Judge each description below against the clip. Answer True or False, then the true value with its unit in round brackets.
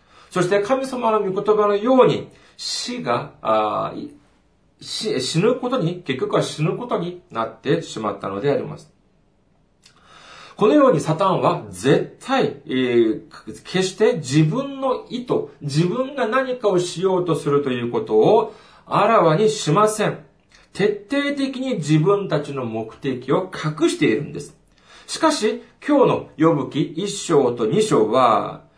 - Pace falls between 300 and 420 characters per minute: False (260 characters per minute)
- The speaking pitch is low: False (185 Hz)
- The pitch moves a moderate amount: False (8.8 semitones)